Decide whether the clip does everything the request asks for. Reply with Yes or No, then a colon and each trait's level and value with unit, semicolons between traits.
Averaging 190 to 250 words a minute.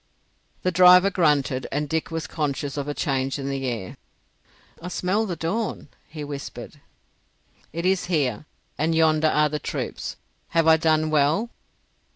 No: average, 155 wpm